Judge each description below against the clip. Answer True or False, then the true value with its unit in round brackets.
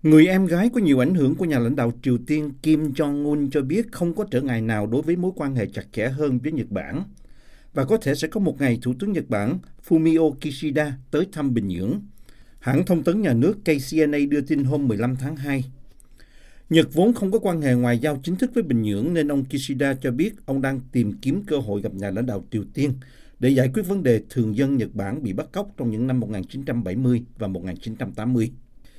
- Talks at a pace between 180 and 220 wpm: False (230 wpm)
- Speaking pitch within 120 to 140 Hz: True (135 Hz)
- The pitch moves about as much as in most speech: True (4.4 semitones)